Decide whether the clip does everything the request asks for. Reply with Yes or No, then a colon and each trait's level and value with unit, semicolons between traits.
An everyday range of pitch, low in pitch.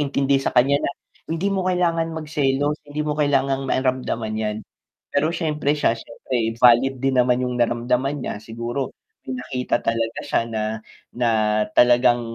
Yes: average, 3.3 semitones; low, 130 Hz